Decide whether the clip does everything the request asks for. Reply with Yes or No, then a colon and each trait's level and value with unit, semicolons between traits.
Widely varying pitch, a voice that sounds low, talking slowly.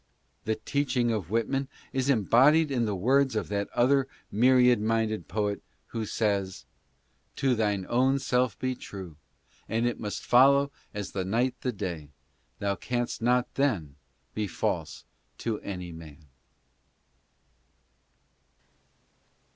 No: average, 4.2 semitones; low, 115 Hz; slow, 130 wpm